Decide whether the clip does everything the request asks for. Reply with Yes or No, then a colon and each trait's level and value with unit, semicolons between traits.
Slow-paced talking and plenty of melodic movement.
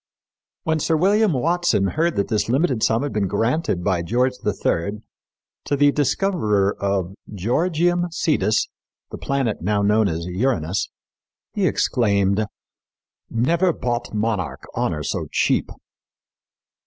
Yes: slow, 125 wpm; wide, 7.5 semitones